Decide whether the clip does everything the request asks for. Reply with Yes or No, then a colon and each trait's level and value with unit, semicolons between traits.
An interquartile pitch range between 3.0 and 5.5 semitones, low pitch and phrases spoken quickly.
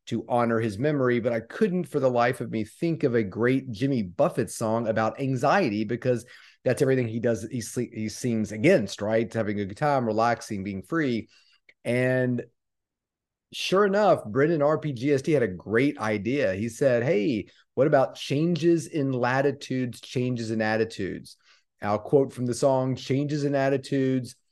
No: average, 3.8 semitones; low, 125 Hz; average, 160 wpm